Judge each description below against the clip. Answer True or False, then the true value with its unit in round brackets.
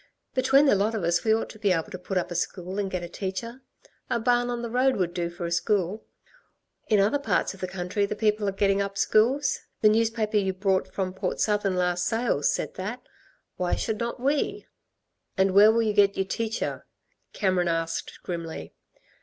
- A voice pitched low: False (200 Hz)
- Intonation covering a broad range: False (3.5 semitones)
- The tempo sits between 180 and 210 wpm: True (205 wpm)